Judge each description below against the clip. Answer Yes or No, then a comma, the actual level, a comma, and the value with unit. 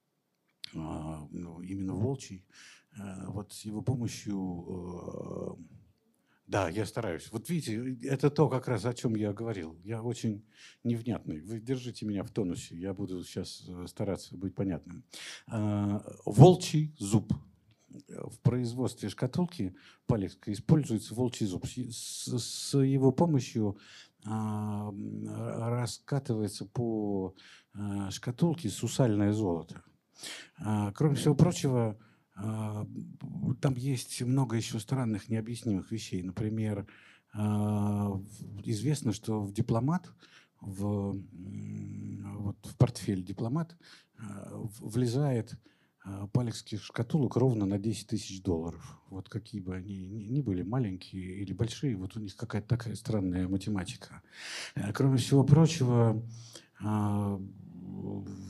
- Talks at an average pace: No, slow, 100 wpm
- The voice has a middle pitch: No, low, 110 Hz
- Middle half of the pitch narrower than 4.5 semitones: Yes, average, 3.8 semitones